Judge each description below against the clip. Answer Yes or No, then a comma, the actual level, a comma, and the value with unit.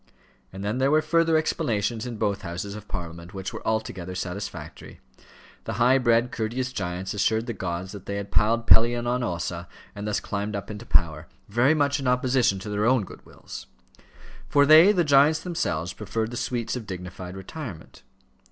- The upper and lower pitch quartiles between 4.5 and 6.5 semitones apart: Yes, average, 4.9 semitones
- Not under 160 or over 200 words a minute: Yes, average, 180 wpm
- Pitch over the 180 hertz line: No, low, 110 Hz